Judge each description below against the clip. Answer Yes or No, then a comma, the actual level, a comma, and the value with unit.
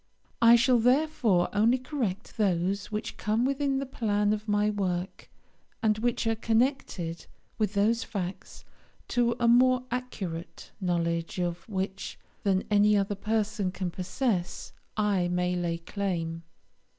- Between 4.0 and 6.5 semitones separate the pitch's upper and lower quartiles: Yes, average, 4.3 semitones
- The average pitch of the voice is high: Yes, high, 205 Hz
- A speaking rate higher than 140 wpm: No, slow, 135 wpm